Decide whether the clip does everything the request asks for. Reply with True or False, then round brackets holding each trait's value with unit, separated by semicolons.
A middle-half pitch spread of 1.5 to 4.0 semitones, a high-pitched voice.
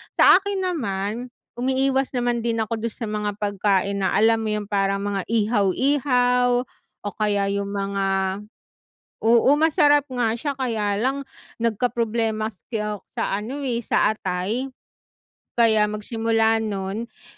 True (3.4 semitones; 225 Hz)